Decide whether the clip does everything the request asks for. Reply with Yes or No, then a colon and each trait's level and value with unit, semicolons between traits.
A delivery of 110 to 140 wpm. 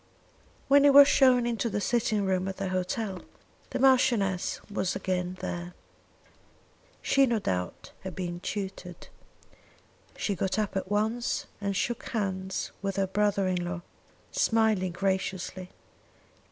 Yes: slow, 135 wpm